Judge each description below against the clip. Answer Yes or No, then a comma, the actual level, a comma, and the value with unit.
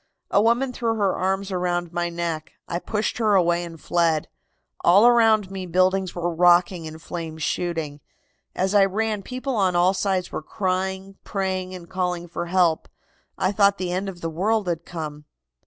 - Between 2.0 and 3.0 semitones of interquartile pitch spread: Yes, narrow, 2.4 semitones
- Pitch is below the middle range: No, medium, 185 Hz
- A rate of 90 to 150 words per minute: No, average, 175 wpm